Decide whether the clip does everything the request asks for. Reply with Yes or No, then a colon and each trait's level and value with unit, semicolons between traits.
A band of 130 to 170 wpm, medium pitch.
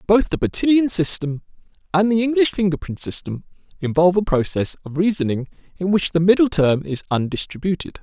Yes: average, 155 wpm; medium, 180 Hz